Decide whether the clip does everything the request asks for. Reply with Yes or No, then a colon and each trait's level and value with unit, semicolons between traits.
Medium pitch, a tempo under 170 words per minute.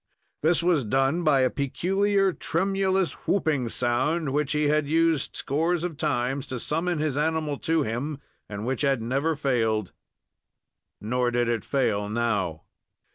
Yes: medium, 145 Hz; average, 145 wpm